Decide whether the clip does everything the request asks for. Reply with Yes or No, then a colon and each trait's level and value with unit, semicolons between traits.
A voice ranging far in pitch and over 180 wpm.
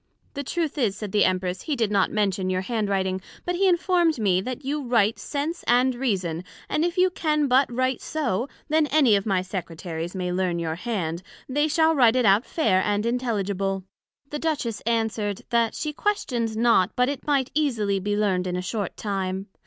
Yes: wide, 6.8 semitones; average, 195 wpm